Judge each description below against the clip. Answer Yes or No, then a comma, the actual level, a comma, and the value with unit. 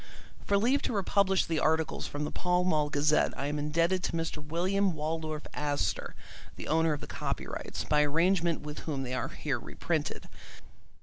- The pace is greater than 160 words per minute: Yes, average, 175 wpm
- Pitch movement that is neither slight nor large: Yes, average, 3.3 semitones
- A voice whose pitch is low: No, medium, 160 Hz